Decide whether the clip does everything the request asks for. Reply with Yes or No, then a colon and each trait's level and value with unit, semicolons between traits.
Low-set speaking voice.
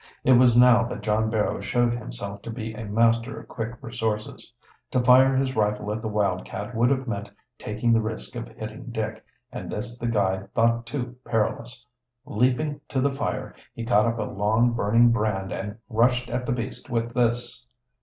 Yes: low, 115 Hz